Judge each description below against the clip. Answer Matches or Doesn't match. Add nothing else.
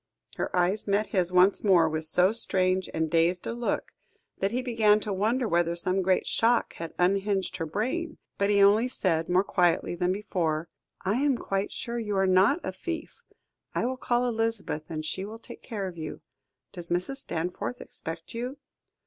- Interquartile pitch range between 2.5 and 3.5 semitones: Doesn't match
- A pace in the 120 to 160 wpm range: Doesn't match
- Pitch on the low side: Doesn't match